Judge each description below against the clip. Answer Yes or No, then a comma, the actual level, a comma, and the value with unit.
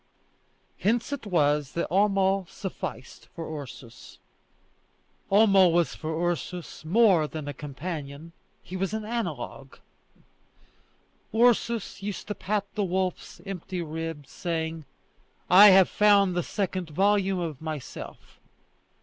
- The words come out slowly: Yes, slow, 115 wpm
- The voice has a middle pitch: Yes, medium, 180 Hz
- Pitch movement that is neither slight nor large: Yes, average, 4.0 semitones